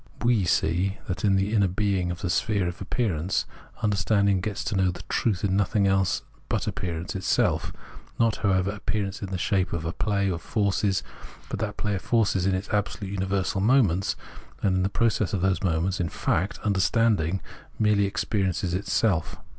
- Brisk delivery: No, average, 175 wpm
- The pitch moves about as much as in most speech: No, narrow, 1.9 semitones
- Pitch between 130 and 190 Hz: No, very low, 95 Hz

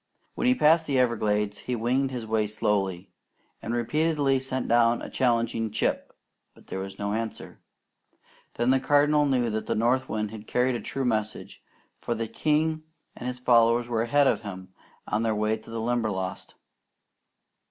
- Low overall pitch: Yes, low, 115 Hz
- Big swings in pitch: No, average, 3.3 semitones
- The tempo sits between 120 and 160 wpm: No, average, 175 wpm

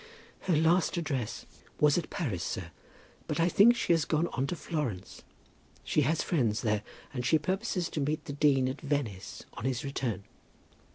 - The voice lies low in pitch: No, medium, 145 Hz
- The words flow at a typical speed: Yes, average, 175 wpm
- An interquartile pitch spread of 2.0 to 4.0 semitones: No, average, 4.9 semitones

